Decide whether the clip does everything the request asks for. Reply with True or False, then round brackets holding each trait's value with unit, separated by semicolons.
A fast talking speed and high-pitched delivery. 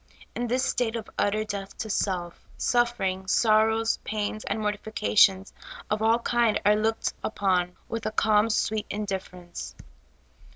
False (135 wpm; 215 Hz)